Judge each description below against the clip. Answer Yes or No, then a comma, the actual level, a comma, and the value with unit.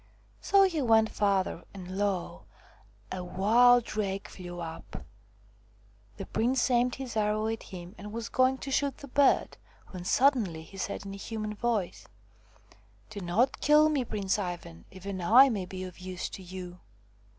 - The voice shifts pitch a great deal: No, average, 5.0 semitones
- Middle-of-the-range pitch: No, high, 205 Hz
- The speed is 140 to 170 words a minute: Yes, average, 165 wpm